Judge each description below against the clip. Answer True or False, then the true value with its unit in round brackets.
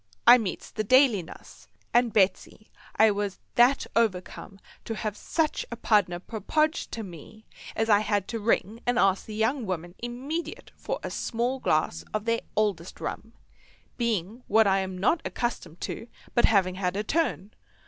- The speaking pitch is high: True (215 Hz)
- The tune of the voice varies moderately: True (3.7 semitones)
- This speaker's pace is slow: False (170 wpm)